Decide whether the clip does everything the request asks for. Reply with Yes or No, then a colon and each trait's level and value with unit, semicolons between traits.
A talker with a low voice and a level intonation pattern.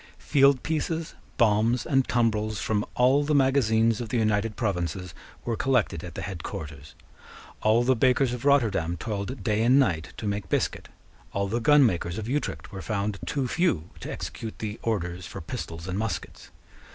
No: low, 110 Hz; average, 4.5 semitones